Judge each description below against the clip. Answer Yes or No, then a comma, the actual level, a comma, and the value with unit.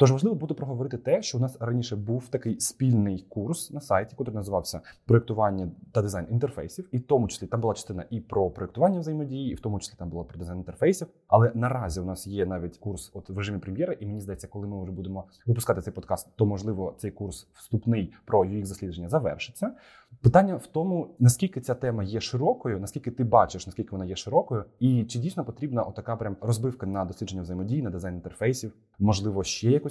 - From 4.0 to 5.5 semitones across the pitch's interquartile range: Yes, average, 4.8 semitones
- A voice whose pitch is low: Yes, low, 110 Hz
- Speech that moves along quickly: Yes, fast, 205 wpm